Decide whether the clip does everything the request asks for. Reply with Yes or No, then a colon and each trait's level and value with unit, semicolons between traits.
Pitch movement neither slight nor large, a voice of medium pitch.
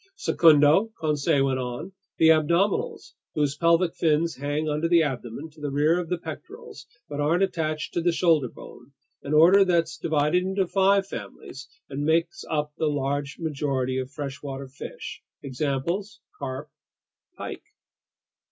Yes: average, 3.3 semitones; medium, 155 Hz